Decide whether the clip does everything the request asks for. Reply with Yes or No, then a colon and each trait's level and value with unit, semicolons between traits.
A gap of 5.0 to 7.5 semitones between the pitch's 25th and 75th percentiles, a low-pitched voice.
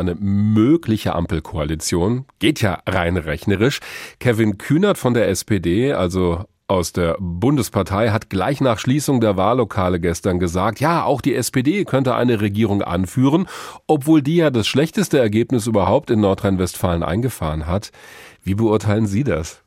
Yes: wide, 5.6 semitones; low, 110 Hz